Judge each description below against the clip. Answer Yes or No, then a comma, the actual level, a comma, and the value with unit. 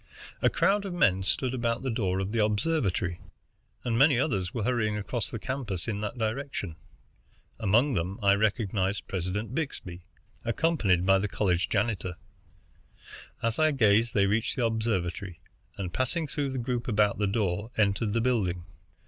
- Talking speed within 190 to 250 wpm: No, average, 160 wpm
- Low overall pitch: Yes, low, 110 Hz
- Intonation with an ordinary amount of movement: Yes, average, 4.1 semitones